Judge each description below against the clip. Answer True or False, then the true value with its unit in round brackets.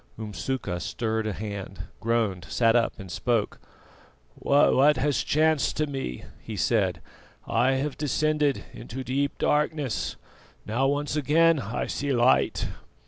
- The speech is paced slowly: True (130 wpm)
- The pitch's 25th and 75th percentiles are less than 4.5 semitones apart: False (4.9 semitones)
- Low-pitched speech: True (130 Hz)